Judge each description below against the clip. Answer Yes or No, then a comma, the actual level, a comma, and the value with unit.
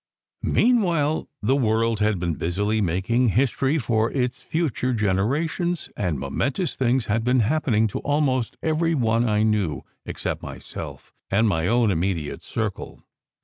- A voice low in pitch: Yes, low, 115 Hz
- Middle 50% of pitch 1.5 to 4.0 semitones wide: No, average, 5.2 semitones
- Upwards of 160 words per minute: No, average, 145 wpm